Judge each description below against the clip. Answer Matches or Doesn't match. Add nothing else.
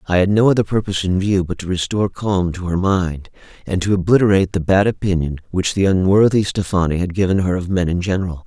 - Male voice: Matches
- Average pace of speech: Doesn't match